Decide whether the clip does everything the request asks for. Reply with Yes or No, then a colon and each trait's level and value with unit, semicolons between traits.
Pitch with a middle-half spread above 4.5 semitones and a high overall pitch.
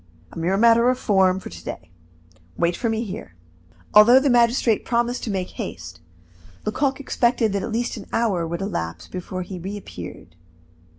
Yes: average, 4.9 semitones; high, 205 Hz